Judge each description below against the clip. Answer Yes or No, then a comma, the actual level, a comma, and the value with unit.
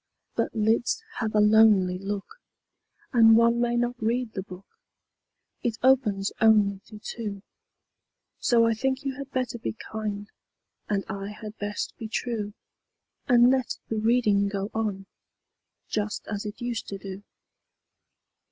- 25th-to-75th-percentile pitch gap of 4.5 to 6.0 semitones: No, average, 2.7 semitones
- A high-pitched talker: Yes, high, 220 Hz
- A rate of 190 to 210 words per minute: No, average, 145 wpm